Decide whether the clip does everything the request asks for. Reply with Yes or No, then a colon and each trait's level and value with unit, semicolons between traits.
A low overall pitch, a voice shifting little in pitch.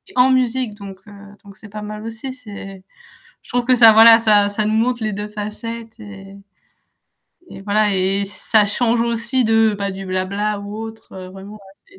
No: high, 215 Hz; narrow, 2.2 semitones